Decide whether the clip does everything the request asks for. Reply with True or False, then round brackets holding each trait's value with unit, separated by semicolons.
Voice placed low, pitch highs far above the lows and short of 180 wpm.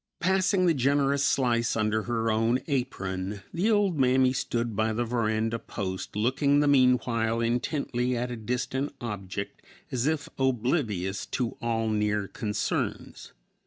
False (120 Hz; 3.5 semitones; 135 wpm)